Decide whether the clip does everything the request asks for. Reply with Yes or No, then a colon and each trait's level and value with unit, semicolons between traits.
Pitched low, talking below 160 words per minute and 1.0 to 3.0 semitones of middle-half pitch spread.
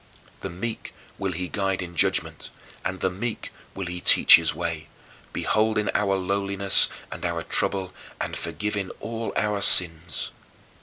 Yes: very low, 95 Hz; average, 150 wpm; narrow, 2.4 semitones